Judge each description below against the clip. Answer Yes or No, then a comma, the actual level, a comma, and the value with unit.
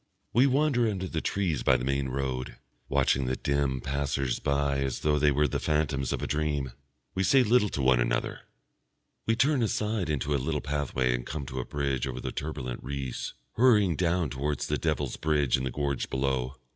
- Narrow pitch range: No, average, 3.7 semitones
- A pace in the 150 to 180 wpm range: No, average, 195 wpm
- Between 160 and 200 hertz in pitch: No, very low, 70 Hz